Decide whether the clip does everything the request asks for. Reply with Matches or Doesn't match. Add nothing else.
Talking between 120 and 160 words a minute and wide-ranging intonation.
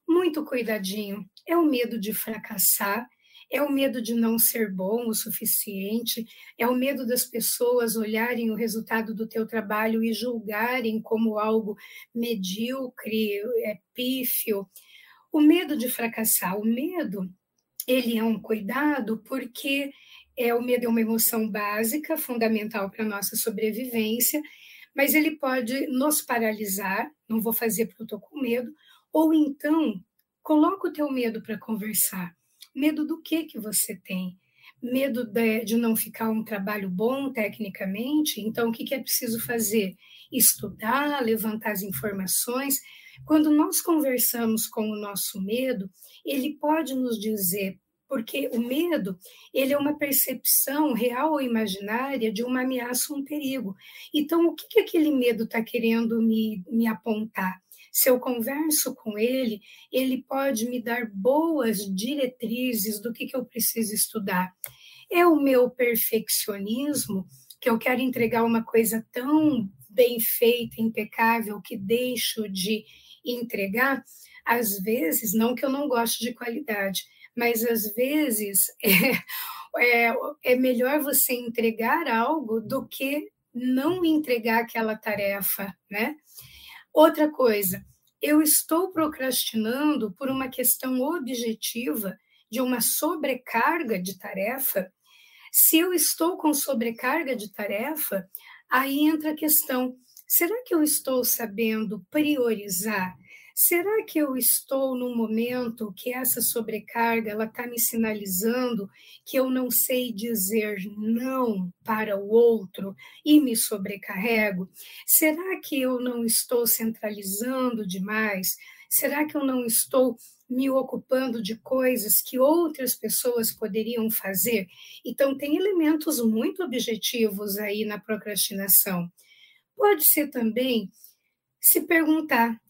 Doesn't match